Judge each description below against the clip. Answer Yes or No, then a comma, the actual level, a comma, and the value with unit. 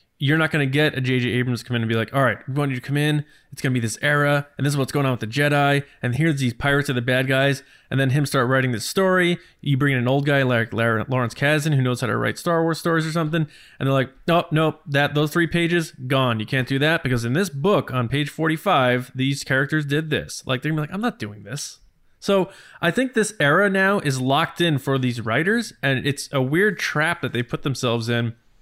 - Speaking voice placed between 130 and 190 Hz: Yes, medium, 140 Hz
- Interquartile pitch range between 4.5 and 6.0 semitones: No, average, 3.6 semitones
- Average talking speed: No, fast, 265 wpm